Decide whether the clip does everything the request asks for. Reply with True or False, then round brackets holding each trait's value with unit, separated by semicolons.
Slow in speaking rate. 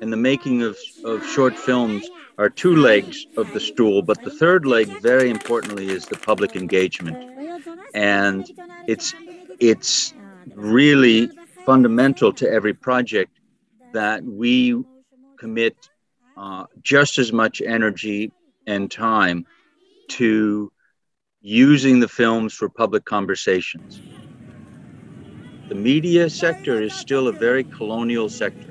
True (120 wpm)